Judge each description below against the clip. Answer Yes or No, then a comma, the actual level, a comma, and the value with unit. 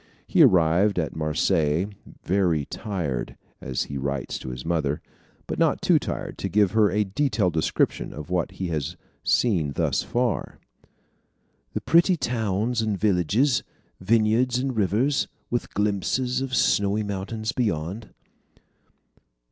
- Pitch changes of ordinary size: No, wide, 5.8 semitones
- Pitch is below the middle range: Yes, low, 100 Hz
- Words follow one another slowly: Yes, slow, 130 wpm